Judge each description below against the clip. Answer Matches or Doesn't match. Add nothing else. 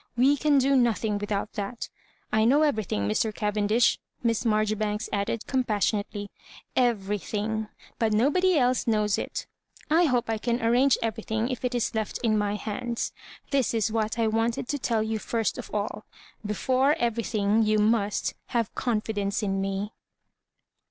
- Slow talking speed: Doesn't match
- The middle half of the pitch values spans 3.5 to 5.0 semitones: Doesn't match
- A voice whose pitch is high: Matches